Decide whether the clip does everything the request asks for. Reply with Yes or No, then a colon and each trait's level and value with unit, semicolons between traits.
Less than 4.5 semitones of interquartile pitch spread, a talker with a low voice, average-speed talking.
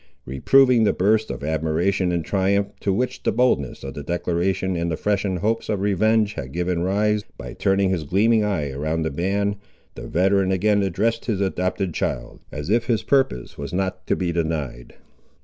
Yes: average, 3.8 semitones; very low, 95 Hz; average, 185 wpm